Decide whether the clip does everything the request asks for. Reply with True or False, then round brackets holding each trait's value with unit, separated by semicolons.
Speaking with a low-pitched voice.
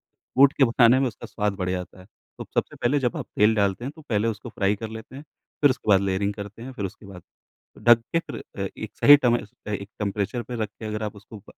True (110 Hz)